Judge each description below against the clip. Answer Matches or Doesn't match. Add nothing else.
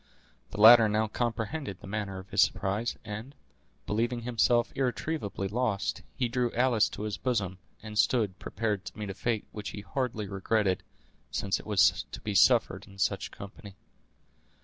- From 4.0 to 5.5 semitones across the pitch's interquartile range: Doesn't match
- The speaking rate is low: Doesn't match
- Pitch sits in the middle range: Doesn't match